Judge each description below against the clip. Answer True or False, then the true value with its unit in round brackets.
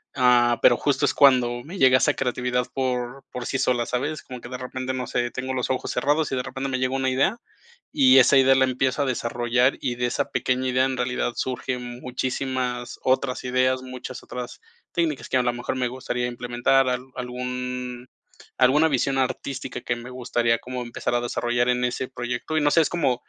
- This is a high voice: False (125 Hz)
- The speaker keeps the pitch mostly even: True (1.2 semitones)